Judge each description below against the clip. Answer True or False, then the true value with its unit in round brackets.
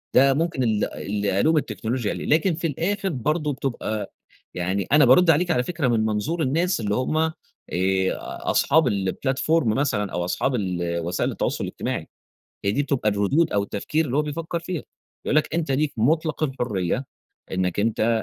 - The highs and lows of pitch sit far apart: True (7.1 semitones)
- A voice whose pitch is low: True (130 Hz)